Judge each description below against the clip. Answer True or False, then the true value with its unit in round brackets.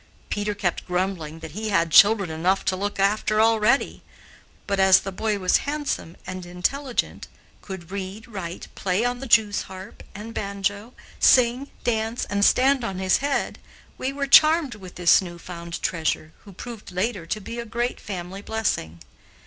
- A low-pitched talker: False (200 Hz)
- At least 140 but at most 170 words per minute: True (165 wpm)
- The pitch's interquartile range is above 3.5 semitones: True (4.1 semitones)